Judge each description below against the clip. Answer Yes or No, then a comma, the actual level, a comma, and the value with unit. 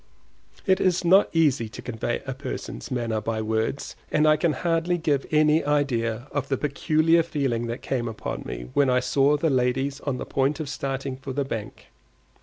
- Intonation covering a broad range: No, average, 3.7 semitones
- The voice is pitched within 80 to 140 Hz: Yes, low, 135 Hz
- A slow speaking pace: No, average, 190 wpm